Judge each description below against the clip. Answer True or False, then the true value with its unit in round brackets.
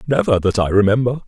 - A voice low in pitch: True (115 Hz)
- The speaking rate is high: False (190 wpm)